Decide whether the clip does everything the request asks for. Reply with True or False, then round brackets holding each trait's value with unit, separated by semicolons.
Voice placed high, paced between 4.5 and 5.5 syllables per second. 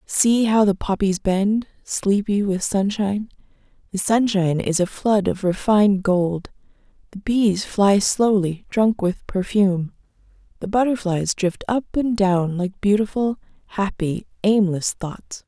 False (200 Hz; 4.0 syllables/s)